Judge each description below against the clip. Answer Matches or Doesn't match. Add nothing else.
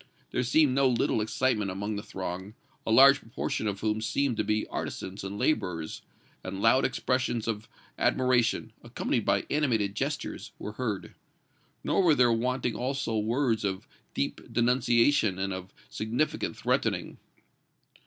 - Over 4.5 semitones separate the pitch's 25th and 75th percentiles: Doesn't match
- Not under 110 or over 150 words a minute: Matches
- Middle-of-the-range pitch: Doesn't match